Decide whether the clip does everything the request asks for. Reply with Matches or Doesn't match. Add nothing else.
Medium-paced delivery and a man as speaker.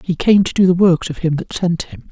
Doesn't match